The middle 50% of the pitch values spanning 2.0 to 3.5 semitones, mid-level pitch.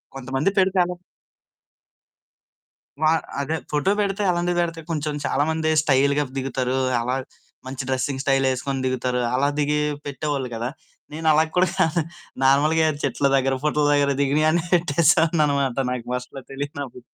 Yes: average, 3.1 semitones; medium, 145 Hz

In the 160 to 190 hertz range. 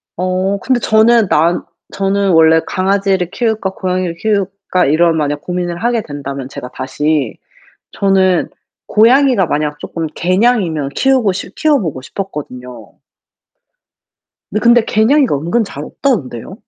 Yes: medium, 185 Hz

